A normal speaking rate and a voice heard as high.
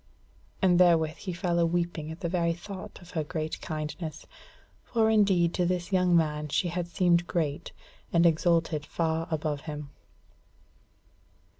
No: average, 150 wpm; medium, 170 Hz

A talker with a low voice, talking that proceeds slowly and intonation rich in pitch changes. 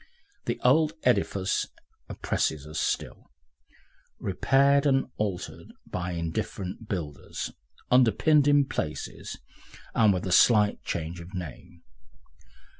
Yes: low, 100 Hz; slow, 105 wpm; wide, 7.0 semitones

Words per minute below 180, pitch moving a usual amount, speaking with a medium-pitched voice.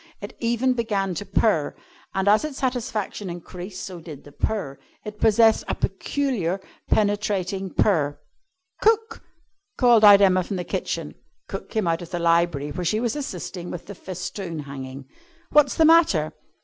No: average, 160 wpm; average, 4.7 semitones; high, 195 Hz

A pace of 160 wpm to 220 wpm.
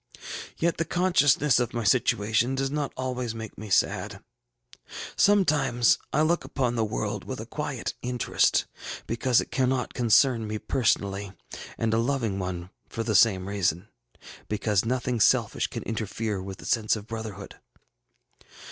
No: average, 145 wpm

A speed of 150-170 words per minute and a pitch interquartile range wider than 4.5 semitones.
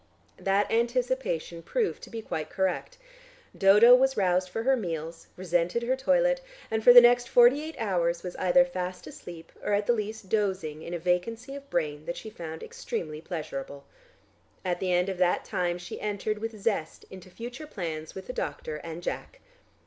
No: average, 180 wpm; wide, 5.5 semitones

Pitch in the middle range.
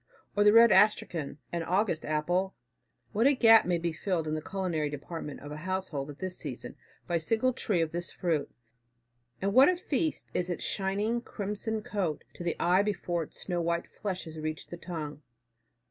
Yes: medium, 180 Hz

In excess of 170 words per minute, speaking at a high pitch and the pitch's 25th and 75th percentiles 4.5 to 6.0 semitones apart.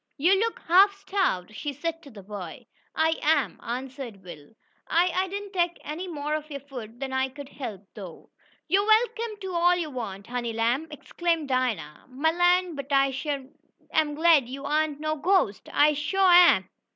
Yes: average, 185 wpm; very high, 295 Hz; wide, 5.6 semitones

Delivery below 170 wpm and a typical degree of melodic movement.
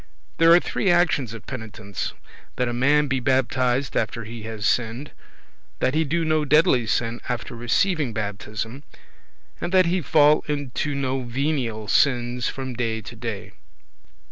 Yes: average, 150 wpm; average, 4.4 semitones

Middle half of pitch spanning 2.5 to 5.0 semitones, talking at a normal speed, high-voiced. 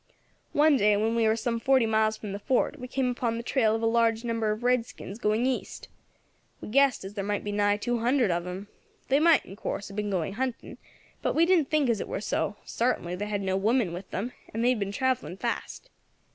No: average, 3.6 semitones; fast, 235 wpm; high, 225 Hz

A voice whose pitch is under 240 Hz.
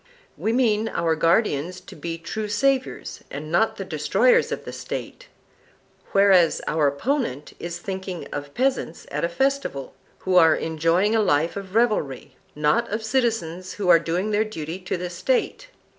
Yes: medium, 185 Hz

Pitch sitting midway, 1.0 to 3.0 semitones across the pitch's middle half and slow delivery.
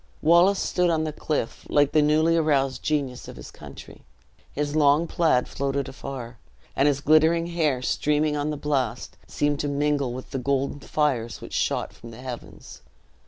No: medium, 145 Hz; narrow, 2.6 semitones; average, 170 wpm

